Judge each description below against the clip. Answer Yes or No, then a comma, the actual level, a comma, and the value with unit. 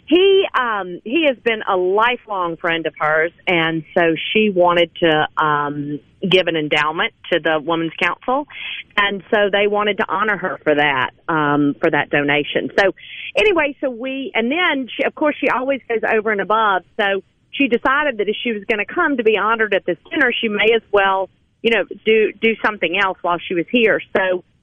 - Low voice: No, high, 200 Hz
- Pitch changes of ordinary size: No, wide, 6.2 semitones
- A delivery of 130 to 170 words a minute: No, average, 200 wpm